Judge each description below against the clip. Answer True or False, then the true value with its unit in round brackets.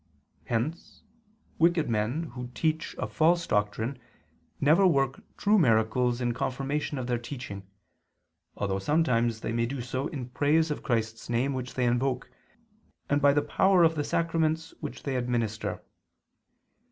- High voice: False (130 Hz)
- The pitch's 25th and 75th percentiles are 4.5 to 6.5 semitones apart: True (4.8 semitones)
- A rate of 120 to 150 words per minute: True (145 wpm)